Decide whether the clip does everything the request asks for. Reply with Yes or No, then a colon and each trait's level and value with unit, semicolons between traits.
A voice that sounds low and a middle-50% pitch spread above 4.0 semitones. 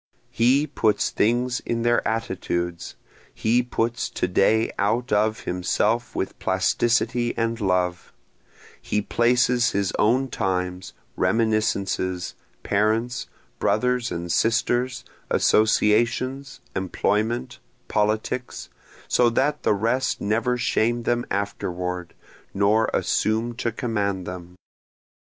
No: low, 110 Hz; average, 3.5 semitones